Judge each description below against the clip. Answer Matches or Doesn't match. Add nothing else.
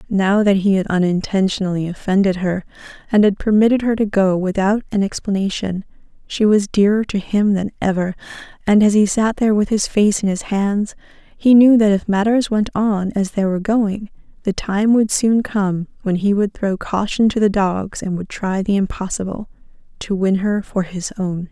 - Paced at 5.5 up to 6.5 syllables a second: Doesn't match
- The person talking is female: Matches